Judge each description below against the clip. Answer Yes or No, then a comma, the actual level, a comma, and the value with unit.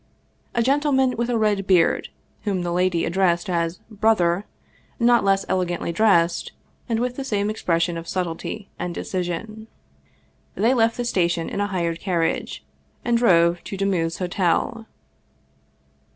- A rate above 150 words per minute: No, average, 145 wpm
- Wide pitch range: No, average, 4.5 semitones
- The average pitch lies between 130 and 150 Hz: No, high, 190 Hz